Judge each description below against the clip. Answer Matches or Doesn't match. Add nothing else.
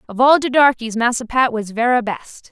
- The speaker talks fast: Matches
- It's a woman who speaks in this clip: Matches